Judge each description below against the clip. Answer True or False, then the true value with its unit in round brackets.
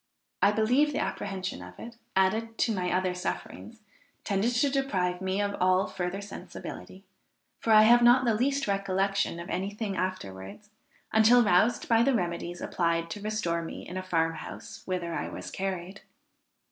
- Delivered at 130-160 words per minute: False (170 wpm)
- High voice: True (195 Hz)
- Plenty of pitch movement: False (3.8 semitones)